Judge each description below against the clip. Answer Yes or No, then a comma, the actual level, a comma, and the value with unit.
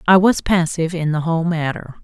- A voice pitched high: No, medium, 165 Hz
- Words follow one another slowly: No, fast, 205 wpm